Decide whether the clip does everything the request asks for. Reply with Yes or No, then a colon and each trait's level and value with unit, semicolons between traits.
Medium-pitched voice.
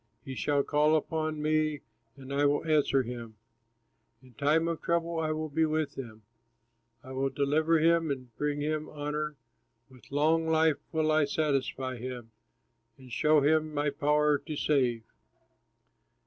Yes: medium, 150 Hz